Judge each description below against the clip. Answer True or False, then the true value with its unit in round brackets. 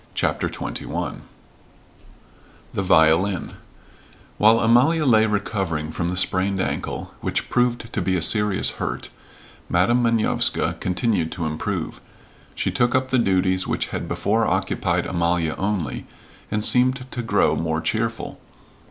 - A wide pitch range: False (4.7 semitones)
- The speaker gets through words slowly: True (130 wpm)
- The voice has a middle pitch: False (100 Hz)